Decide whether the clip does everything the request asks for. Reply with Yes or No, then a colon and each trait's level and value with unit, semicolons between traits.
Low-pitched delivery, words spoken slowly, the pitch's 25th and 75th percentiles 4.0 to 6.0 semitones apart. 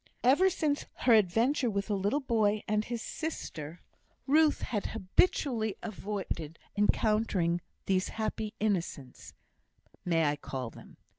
No: high, 210 Hz; slow, 125 wpm; average, 4.5 semitones